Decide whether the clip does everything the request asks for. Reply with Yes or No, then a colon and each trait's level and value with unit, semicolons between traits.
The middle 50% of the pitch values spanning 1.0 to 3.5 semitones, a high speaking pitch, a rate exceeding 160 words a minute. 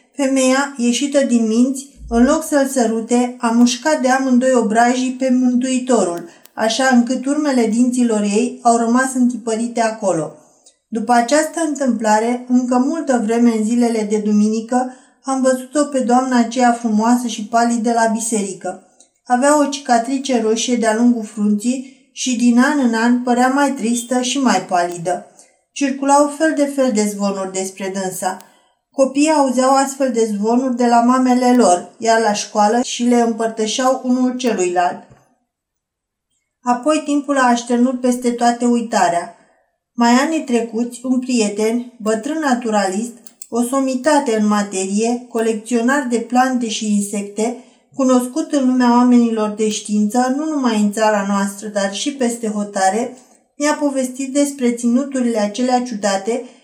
No: average, 2.7 semitones; high, 240 Hz; average, 140 wpm